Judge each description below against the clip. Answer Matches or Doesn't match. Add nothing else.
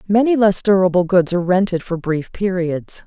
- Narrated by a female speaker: Matches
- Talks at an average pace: Matches